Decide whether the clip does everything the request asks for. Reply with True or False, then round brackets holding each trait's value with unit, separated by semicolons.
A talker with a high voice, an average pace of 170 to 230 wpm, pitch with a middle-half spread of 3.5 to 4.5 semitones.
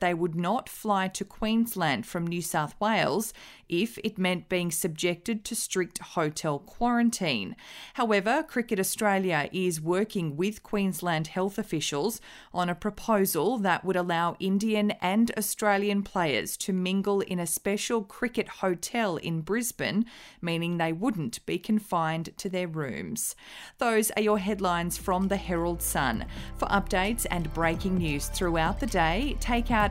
False (195 Hz; 145 wpm; 3.9 semitones)